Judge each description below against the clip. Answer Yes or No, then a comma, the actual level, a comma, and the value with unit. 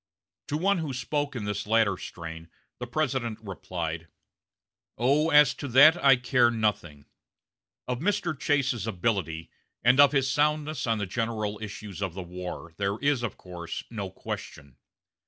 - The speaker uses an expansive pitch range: Yes, wide, 6.6 semitones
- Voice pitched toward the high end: No, low, 115 Hz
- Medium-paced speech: Yes, average, 155 wpm